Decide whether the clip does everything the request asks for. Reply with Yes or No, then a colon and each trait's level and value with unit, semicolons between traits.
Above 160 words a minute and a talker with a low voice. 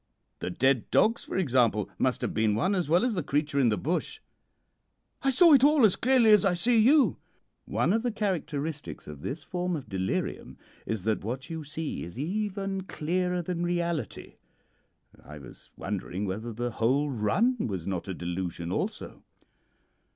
No: average, 175 wpm; medium, 155 Hz